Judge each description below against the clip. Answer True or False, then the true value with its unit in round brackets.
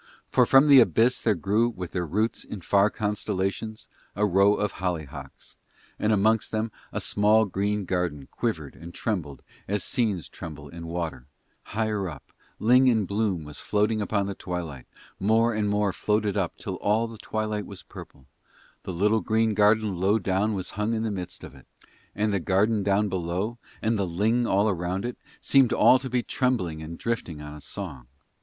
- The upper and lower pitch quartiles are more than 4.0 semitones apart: False (3.6 semitones)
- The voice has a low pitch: True (100 Hz)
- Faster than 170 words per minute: True (180 wpm)